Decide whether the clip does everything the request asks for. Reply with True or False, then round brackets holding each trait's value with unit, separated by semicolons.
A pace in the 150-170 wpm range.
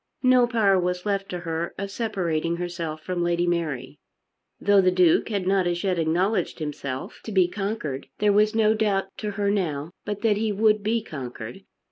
False (185 wpm)